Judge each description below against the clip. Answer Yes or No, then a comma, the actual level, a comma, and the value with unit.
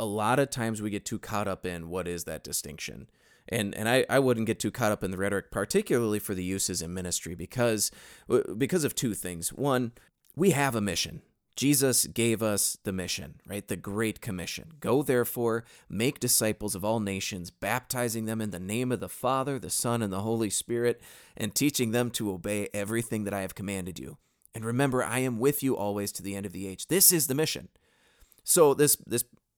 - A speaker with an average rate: No, fast, 210 wpm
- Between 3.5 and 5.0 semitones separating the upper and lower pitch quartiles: Yes, average, 3.9 semitones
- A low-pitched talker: Yes, low, 110 Hz